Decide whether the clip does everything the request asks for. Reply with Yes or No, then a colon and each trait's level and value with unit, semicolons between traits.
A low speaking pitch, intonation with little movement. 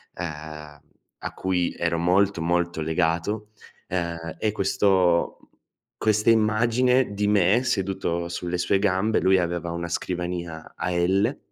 No: very low, 90 Hz; average, 3.2 semitones